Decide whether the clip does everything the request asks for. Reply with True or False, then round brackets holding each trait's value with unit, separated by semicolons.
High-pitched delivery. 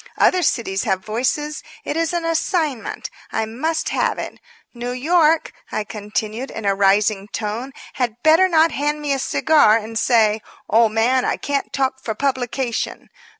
True (250 Hz)